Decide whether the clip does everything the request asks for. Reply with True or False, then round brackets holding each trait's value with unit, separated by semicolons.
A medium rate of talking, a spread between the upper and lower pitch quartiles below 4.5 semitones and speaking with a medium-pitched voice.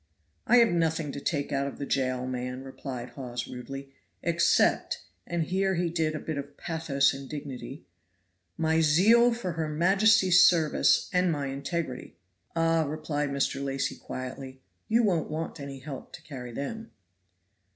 True (155 wpm; 3.8 semitones; 150 Hz)